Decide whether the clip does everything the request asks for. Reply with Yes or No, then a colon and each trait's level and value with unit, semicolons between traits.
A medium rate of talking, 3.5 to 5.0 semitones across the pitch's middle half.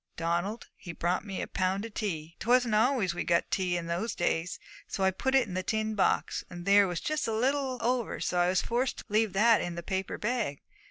No: fast, 230 wpm; average, 4.7 semitones